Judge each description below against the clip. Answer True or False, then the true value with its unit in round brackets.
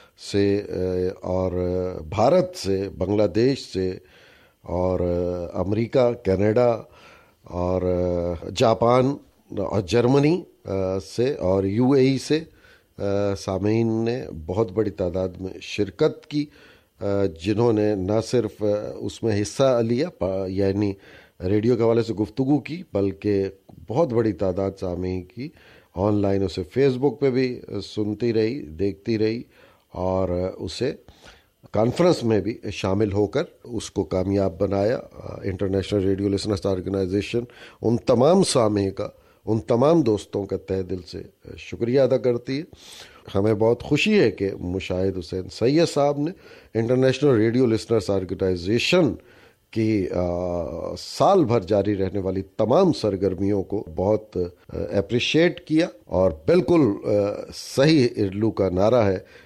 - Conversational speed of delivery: True (125 wpm)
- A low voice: True (105 Hz)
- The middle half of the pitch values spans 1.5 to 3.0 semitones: False (3.8 semitones)